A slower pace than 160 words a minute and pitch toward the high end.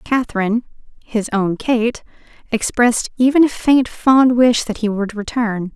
Yes: average, 145 wpm; high, 230 Hz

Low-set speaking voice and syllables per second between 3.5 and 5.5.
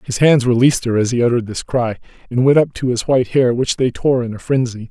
No: low, 125 Hz; 6.3 syllables/s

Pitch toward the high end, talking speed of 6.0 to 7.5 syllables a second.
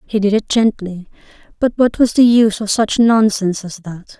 No: high, 210 Hz; 5.1 syllables/s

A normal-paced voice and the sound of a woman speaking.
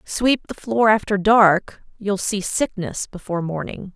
Yes: average, 150 wpm; female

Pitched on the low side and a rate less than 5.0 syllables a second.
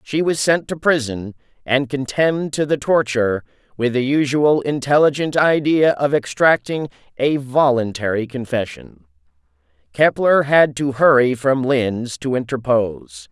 Yes: low, 130 Hz; 4.4 syllables/s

